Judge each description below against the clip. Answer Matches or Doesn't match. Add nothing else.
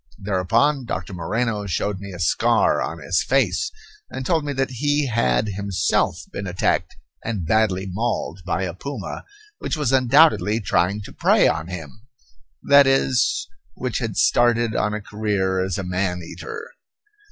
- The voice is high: Doesn't match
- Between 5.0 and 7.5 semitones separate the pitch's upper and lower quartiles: Matches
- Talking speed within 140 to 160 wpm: Matches